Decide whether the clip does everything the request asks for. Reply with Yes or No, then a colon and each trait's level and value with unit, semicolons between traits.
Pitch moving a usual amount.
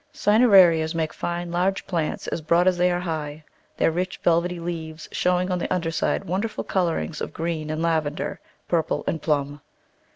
No: narrow, 2.2 semitones